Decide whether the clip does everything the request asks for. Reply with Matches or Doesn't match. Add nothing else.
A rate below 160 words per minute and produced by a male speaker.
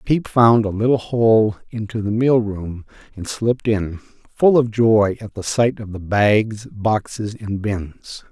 Doesn't match